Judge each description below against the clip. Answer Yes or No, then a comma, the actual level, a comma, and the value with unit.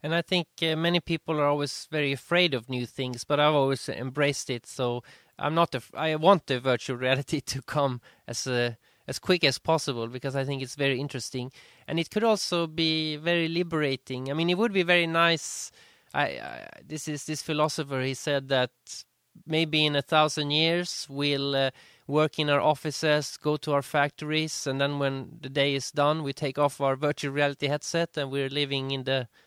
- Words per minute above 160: Yes, average, 200 wpm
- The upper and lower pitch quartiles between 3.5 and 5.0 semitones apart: No, average, 2.7 semitones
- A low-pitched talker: No, medium, 145 Hz